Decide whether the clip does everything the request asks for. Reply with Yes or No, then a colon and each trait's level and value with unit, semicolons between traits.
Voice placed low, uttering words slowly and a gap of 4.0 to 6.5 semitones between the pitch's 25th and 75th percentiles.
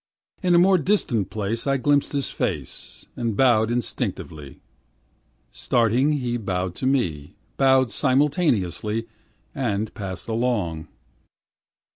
Yes: low, 120 Hz; slow, 110 wpm; average, 5.1 semitones